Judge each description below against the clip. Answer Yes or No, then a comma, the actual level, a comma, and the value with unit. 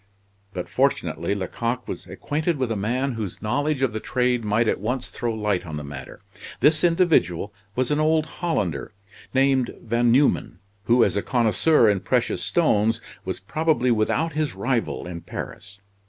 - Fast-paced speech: No, average, 165 wpm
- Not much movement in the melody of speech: No, average, 5.2 semitones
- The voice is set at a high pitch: No, low, 120 Hz